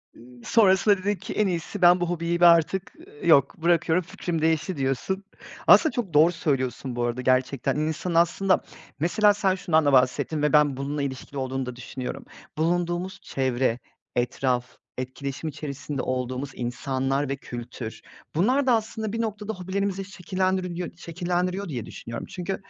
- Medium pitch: Yes, medium, 160 Hz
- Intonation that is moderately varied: No, wide, 5.8 semitones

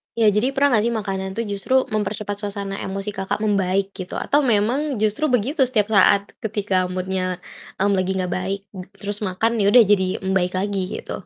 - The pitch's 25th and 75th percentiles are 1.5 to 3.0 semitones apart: Yes, narrow, 2.4 semitones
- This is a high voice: Yes, high, 205 Hz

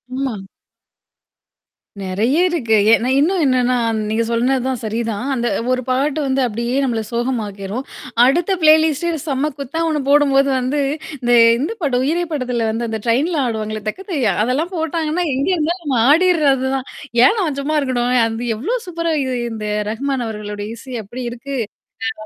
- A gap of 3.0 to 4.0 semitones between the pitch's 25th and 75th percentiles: No, average, 4.6 semitones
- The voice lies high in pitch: Yes, very high, 260 Hz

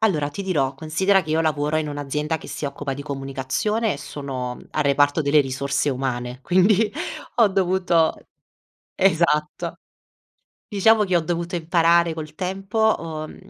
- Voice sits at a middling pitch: Yes, medium, 155 Hz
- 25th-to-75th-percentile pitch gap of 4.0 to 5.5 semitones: Yes, average, 4.6 semitones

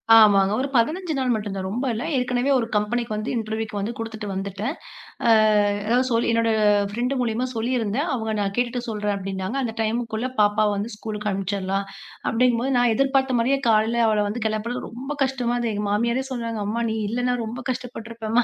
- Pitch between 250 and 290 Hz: No, high, 225 Hz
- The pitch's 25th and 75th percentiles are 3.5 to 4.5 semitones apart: No, average, 2.7 semitones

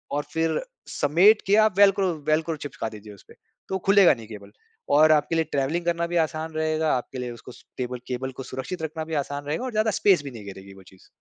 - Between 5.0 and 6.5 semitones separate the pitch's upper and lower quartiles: Yes, average, 5.3 semitones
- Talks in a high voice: No, medium, 155 Hz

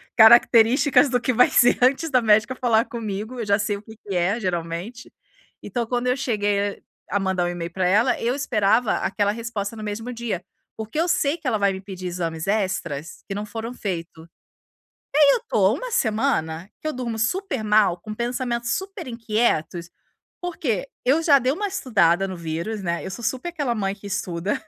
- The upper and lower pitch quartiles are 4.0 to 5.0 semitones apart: Yes, average, 4.4 semitones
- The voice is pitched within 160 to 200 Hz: No, high, 220 Hz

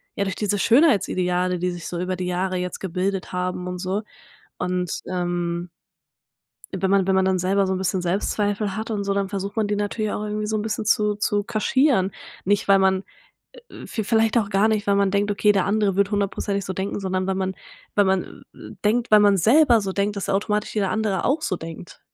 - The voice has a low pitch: No, high, 200 Hz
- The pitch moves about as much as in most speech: No, narrow, 2.1 semitones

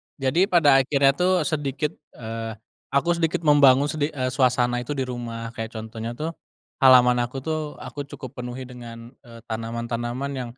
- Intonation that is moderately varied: Yes, average, 3.4 semitones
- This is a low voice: Yes, low, 130 Hz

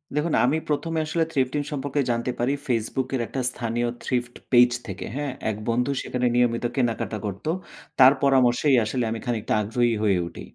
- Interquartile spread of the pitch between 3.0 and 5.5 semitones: No, narrow, 2.6 semitones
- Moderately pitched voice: No, low, 125 Hz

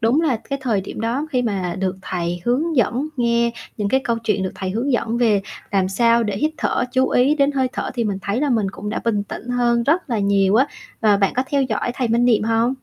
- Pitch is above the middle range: Yes, high, 235 Hz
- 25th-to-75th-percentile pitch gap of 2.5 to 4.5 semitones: Yes, average, 3.9 semitones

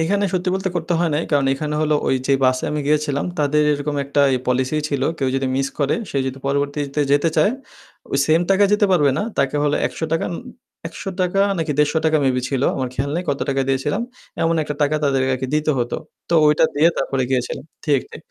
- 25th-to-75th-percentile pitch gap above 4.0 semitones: No, average, 2.9 semitones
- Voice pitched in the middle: Yes, medium, 145 Hz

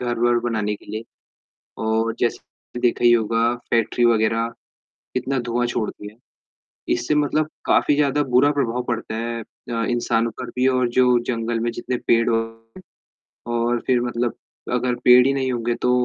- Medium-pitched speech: No, low, 120 Hz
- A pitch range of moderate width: No, narrow, 1.6 semitones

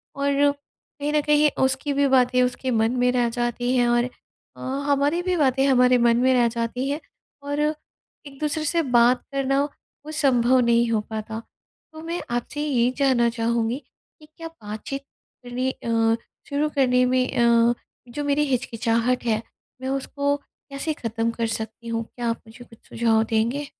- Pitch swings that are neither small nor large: Yes, average, 3.2 semitones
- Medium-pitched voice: No, very high, 250 Hz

